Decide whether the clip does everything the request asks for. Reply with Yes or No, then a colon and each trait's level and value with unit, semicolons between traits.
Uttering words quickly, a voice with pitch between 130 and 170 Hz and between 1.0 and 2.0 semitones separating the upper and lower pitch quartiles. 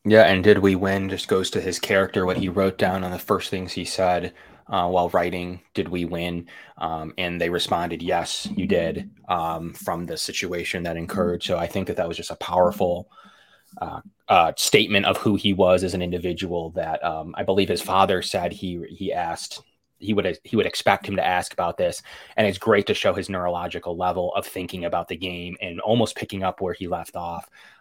No: fast, 215 wpm; very low, 90 Hz; narrow, 1.6 semitones